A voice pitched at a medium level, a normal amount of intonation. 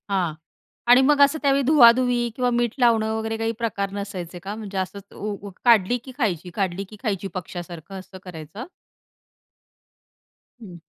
No: high, 210 Hz; average, 4.2 semitones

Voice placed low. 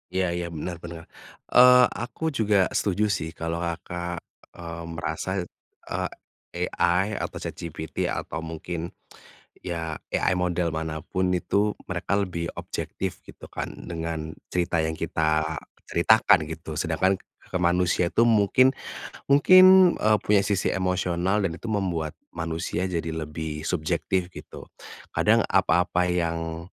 Yes: very low, 85 Hz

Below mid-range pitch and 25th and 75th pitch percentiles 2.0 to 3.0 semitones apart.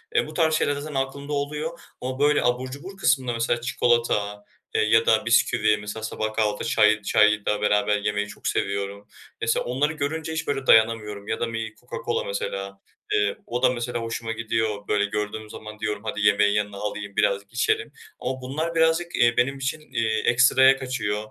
No: low, 115 Hz; average, 4.2 semitones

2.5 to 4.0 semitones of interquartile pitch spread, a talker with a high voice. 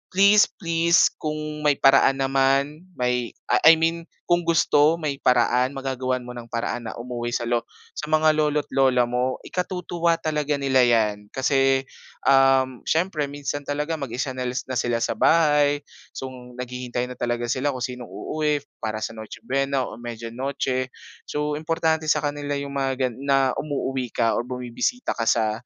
No: average, 3.3 semitones; low, 135 Hz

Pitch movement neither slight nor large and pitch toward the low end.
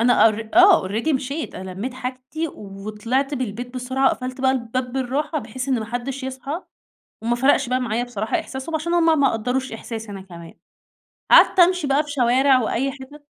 No: average, 3.2 semitones; very high, 255 Hz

